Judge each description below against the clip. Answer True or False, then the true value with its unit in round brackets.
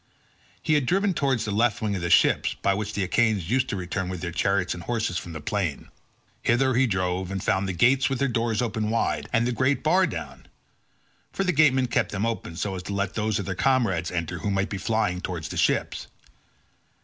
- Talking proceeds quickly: True (225 wpm)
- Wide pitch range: False (4.9 semitones)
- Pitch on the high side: False (105 Hz)